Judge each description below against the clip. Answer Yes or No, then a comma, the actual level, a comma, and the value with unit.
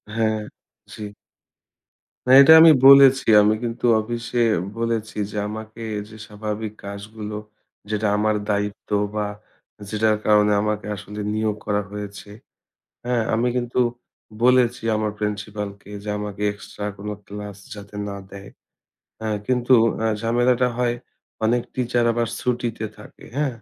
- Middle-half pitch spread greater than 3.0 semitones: No, narrow, 2.4 semitones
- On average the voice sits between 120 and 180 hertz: No, low, 110 Hz